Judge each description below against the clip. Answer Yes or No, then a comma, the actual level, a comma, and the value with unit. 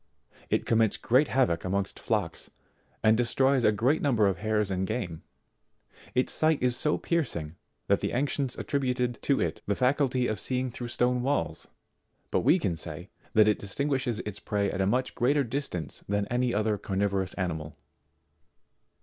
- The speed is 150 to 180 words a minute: Yes, average, 165 wpm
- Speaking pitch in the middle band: No, low, 120 Hz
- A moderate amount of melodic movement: Yes, average, 4.6 semitones